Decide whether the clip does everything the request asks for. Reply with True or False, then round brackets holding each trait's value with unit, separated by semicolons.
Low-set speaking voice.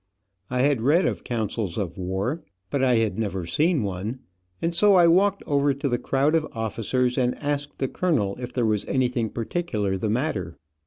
True (125 Hz)